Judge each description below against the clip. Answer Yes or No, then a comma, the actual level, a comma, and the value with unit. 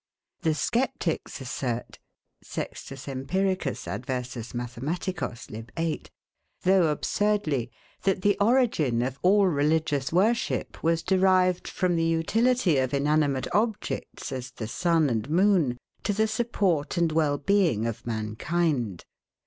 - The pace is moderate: No, slow, 120 wpm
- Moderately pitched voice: Yes, medium, 160 Hz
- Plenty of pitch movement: Yes, wide, 6.4 semitones